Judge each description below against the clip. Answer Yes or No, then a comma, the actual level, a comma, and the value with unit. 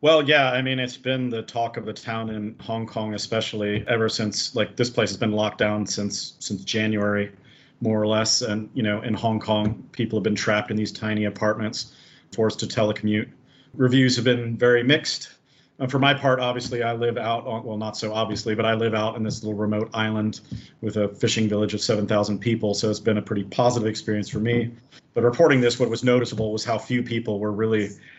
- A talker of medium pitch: No, low, 110 Hz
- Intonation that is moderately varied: No, narrow, 2.1 semitones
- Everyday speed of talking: No, fast, 215 wpm